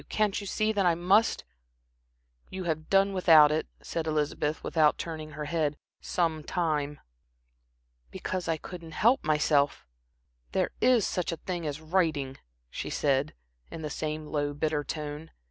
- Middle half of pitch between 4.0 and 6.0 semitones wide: No, average, 3.1 semitones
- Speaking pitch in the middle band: Yes, medium, 160 Hz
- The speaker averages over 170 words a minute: No, average, 150 wpm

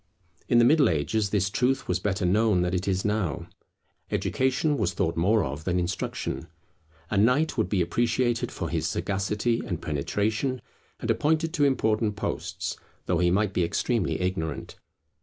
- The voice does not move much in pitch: No, average, 5.2 semitones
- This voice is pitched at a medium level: No, low, 105 Hz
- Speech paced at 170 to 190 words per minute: No, average, 160 wpm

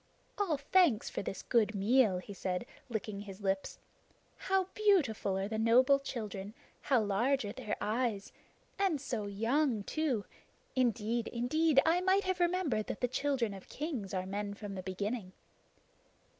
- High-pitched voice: Yes, high, 230 Hz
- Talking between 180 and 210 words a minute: No, average, 155 wpm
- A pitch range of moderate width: No, wide, 5.7 semitones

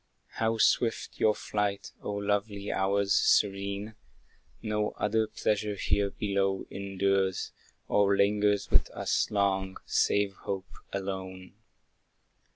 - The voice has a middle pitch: No, low, 100 Hz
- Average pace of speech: No, slow, 105 wpm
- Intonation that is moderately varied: No, narrow, 1.1 semitones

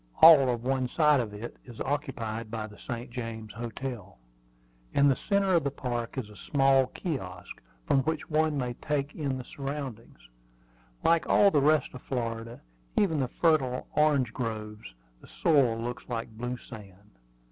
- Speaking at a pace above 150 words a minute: Yes, average, 165 wpm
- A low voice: Yes, low, 125 Hz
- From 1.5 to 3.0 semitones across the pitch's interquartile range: No, average, 4.1 semitones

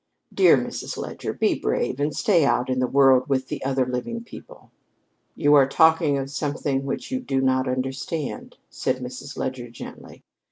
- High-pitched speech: No, low, 135 Hz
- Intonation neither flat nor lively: No, narrow, 2.3 semitones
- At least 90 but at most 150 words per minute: No, average, 170 wpm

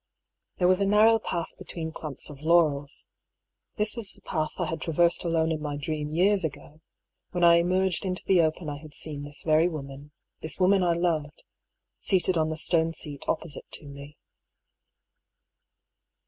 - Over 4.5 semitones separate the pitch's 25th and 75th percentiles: No, average, 3.1 semitones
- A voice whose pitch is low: No, medium, 160 Hz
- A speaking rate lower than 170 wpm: No, average, 175 wpm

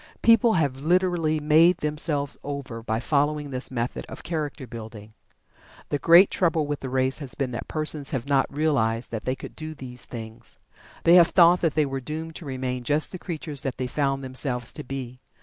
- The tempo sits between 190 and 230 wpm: Yes, average, 195 wpm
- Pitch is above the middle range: No, medium, 140 Hz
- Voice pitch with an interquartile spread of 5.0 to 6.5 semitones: No, average, 3.5 semitones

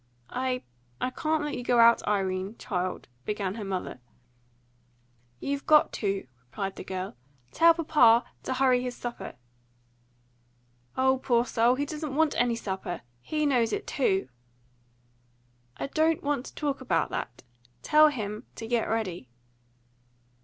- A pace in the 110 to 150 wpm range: Yes, average, 140 wpm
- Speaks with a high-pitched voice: Yes, high, 245 Hz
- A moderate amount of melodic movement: No, wide, 5.8 semitones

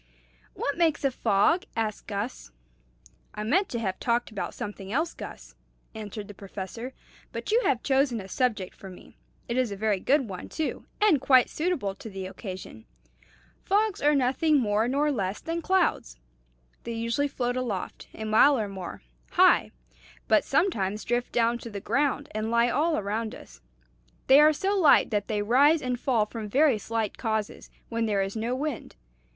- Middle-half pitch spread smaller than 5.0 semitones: No, wide, 5.4 semitones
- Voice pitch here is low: No, high, 235 Hz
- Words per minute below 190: Yes, average, 175 wpm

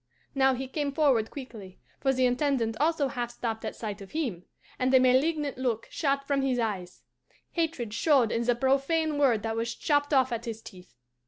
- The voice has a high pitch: Yes, very high, 255 Hz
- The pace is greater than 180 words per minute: Yes, average, 190 wpm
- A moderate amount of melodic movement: Yes, average, 3.7 semitones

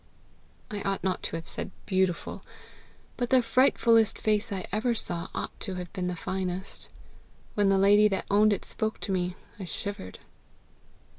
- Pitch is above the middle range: Yes, high, 195 Hz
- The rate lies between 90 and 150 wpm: No, average, 165 wpm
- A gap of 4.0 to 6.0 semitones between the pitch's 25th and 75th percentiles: No, average, 2.7 semitones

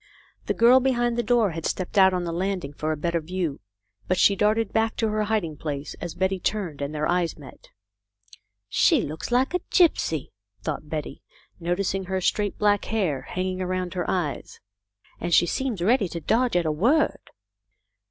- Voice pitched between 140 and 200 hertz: Yes, medium, 185 Hz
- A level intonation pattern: No, average, 4.8 semitones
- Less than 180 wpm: No, average, 185 wpm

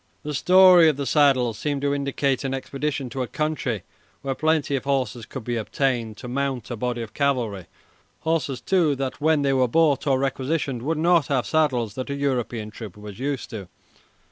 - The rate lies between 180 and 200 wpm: Yes, average, 195 wpm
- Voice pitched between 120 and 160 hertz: Yes, low, 135 Hz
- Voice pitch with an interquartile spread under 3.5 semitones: Yes, average, 3.1 semitones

